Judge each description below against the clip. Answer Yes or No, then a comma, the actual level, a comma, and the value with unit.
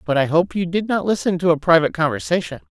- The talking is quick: Yes, fast, 245 wpm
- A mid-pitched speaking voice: Yes, medium, 170 Hz